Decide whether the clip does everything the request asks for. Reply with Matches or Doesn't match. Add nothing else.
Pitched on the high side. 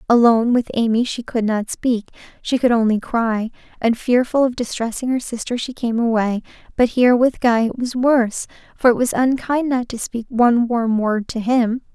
Matches